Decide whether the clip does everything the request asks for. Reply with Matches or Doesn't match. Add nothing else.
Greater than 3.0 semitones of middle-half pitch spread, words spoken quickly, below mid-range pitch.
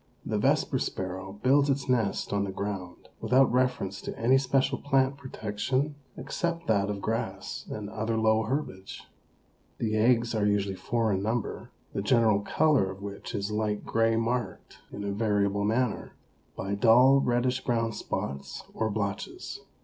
Doesn't match